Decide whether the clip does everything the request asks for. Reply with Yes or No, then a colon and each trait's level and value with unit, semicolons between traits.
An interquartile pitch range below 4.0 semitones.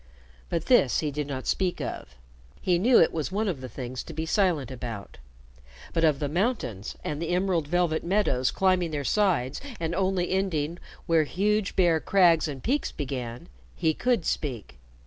No: average, 4.9 semitones